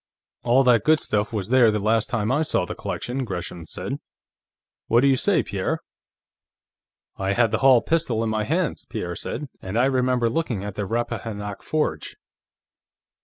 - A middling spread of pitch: Yes, average, 4.0 semitones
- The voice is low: Yes, low, 115 Hz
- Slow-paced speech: No, average, 170 wpm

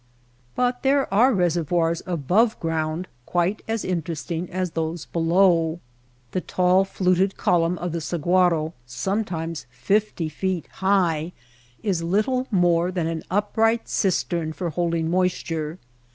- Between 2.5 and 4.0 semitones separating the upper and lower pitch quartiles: Yes, average, 2.8 semitones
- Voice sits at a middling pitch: Yes, medium, 175 Hz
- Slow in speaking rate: Yes, slow, 125 wpm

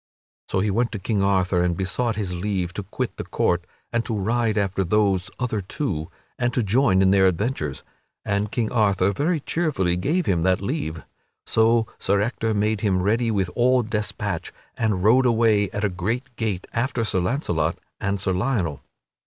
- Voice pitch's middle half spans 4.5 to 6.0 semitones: No, average, 3.9 semitones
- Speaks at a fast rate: No, average, 180 wpm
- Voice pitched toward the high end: No, low, 105 Hz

